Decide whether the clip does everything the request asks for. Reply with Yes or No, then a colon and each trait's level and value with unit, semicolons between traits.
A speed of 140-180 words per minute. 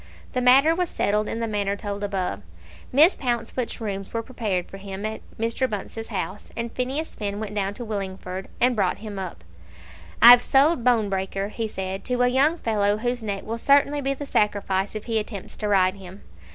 No: average, 190 wpm